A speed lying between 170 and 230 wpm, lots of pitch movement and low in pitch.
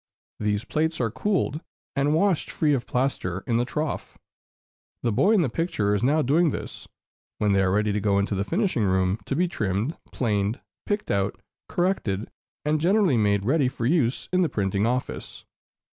Yes: average, 180 wpm; wide, 7.5 semitones; low, 125 Hz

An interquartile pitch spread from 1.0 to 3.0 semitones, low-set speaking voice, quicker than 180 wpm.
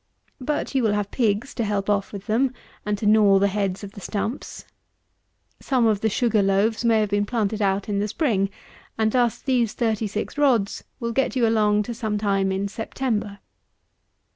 No: narrow, 2.5 semitones; high, 215 Hz; average, 190 wpm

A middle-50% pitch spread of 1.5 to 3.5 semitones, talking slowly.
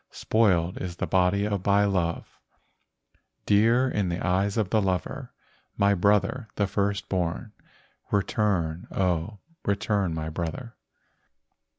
Yes: average, 2.7 semitones; slow, 115 wpm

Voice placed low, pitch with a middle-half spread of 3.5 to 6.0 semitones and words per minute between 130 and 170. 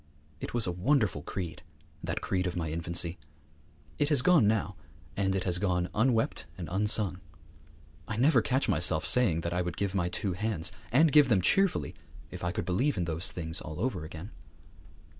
No: very low, 95 Hz; average, 4.6 semitones; average, 185 wpm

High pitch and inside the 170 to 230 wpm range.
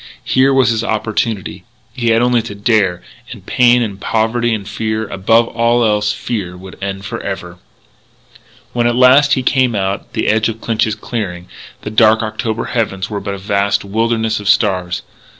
No: low, 110 Hz; average, 175 wpm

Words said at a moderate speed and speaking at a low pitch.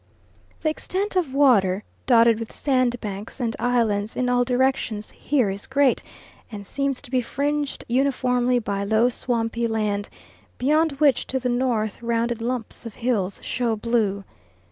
No: average, 145 wpm; high, 240 Hz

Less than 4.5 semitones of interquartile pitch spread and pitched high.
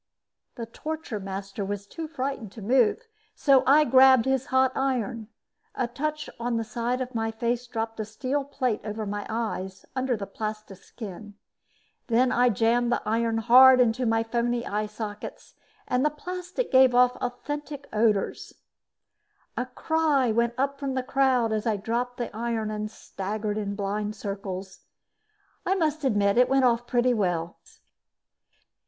Yes: average, 3.6 semitones; high, 235 Hz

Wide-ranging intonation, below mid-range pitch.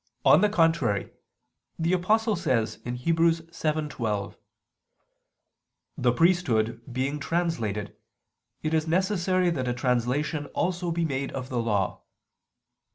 No: wide, 5.7 semitones; medium, 155 Hz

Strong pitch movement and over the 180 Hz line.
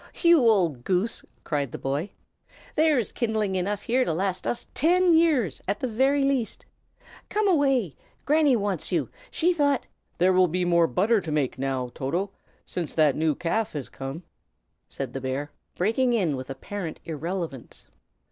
Yes: wide, 8.6 semitones; high, 190 Hz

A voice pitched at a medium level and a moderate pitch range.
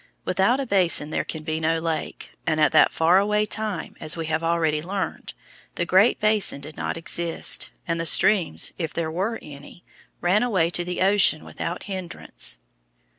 Yes: medium, 170 Hz; average, 3.4 semitones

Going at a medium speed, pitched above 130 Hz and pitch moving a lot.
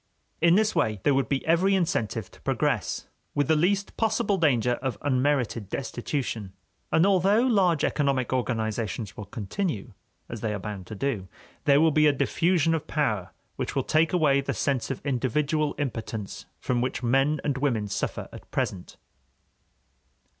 Yes: average, 160 wpm; medium, 140 Hz; wide, 6.0 semitones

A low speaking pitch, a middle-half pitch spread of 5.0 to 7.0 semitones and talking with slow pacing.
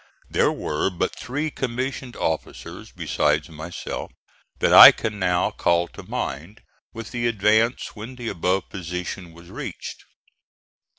Yes: very low, 95 Hz; wide, 5.5 semitones; slow, 130 wpm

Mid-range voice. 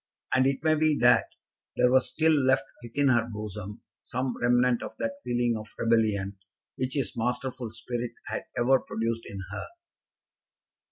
No: low, 120 Hz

